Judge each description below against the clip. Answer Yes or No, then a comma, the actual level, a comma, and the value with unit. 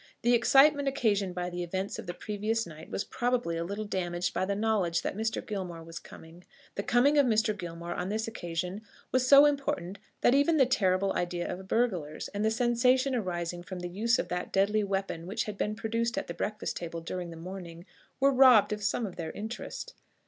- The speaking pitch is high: Yes, high, 200 Hz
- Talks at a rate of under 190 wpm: No, fast, 205 wpm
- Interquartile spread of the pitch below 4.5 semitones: No, average, 4.9 semitones